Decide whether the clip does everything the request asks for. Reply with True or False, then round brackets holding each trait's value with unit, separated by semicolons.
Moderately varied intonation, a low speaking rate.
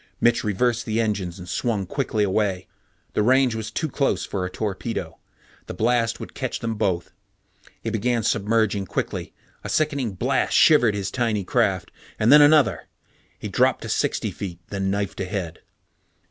False (3.5 semitones; 160 wpm)